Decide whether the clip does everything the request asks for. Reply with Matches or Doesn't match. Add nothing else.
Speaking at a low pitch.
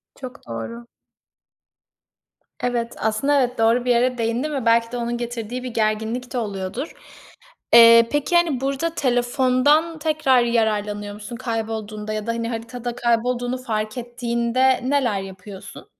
Doesn't match